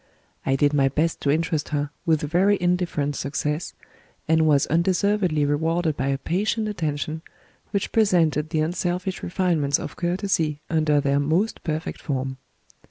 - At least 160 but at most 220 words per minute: No, average, 145 wpm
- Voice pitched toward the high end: No, medium, 160 Hz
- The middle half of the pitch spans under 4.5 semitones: Yes, average, 3.4 semitones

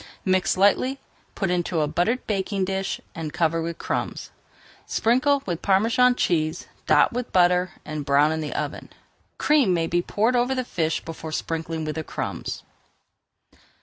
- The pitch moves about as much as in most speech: No, wide, 5.7 semitones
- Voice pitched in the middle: Yes, medium, 180 Hz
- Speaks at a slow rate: No, average, 150 wpm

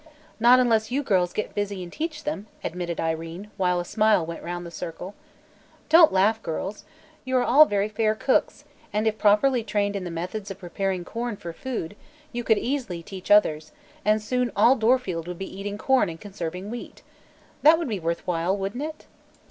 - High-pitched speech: Yes, high, 205 Hz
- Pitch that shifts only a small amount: No, average, 5.1 semitones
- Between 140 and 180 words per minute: No, average, 190 wpm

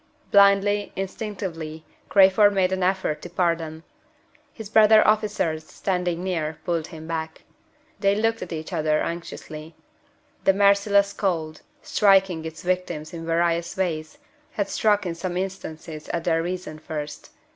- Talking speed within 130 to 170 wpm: Yes, average, 140 wpm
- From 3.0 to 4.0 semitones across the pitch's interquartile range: Yes, average, 3.6 semitones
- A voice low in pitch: No, medium, 180 Hz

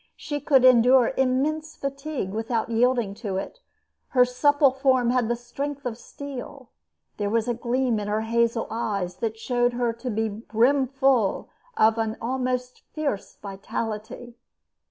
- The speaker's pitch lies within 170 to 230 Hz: No, high, 240 Hz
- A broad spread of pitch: No, average, 2.9 semitones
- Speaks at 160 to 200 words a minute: No, average, 145 wpm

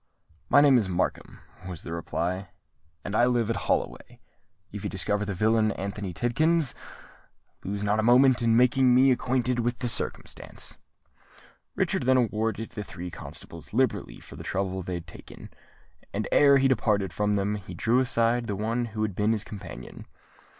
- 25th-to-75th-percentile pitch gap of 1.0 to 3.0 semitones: No, average, 3.7 semitones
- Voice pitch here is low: Yes, low, 110 Hz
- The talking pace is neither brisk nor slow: Yes, average, 170 wpm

